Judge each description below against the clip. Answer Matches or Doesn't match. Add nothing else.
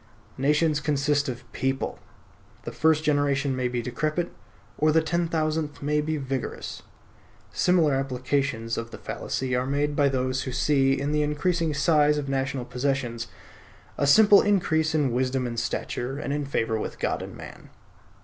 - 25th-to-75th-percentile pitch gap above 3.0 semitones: Doesn't match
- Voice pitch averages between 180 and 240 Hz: Doesn't match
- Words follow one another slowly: Doesn't match